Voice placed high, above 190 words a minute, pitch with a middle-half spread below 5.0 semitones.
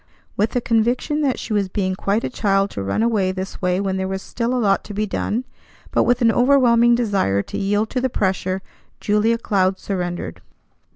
Yes: high, 205 Hz; fast, 205 wpm; average, 3.7 semitones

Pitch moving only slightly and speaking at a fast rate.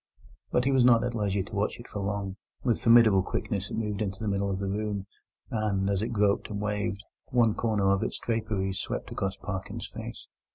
Yes: narrow, 2.3 semitones; fast, 210 wpm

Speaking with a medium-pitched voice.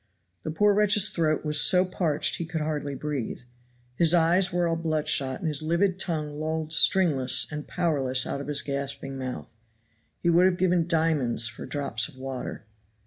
Yes: medium, 155 Hz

